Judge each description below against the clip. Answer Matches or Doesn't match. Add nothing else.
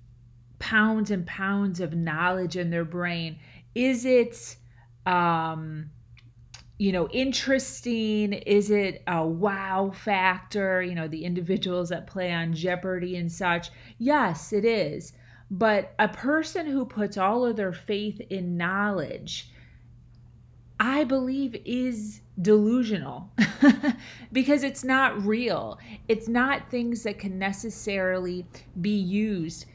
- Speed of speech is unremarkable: Doesn't match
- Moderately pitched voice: Doesn't match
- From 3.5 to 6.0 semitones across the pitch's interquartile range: Matches